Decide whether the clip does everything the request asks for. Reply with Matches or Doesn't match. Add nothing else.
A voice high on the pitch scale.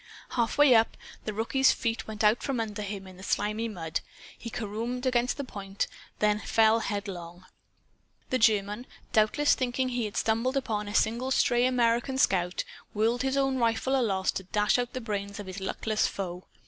Matches